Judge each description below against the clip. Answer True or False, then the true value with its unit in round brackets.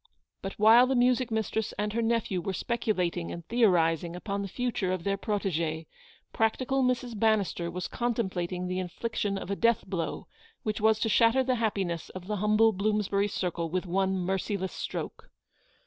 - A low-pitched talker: False (200 Hz)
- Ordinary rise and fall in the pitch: True (3.6 semitones)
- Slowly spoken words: False (165 wpm)